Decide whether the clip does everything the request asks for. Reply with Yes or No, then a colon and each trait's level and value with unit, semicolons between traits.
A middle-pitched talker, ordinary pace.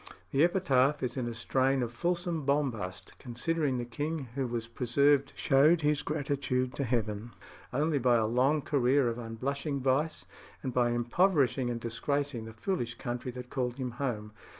No: low, 130 Hz; average, 165 wpm